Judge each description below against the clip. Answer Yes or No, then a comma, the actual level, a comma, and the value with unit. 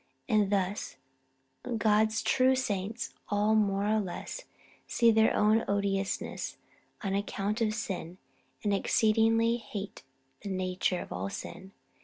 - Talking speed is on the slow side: Yes, slow, 125 wpm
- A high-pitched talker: Yes, high, 210 Hz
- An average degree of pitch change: No, narrow, 2.1 semitones